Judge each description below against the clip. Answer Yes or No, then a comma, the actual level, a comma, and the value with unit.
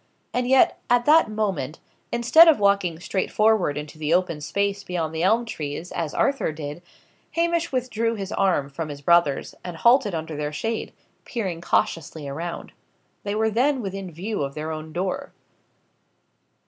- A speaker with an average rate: Yes, average, 160 wpm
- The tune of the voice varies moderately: No, wide, 6.1 semitones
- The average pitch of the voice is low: No, medium, 185 Hz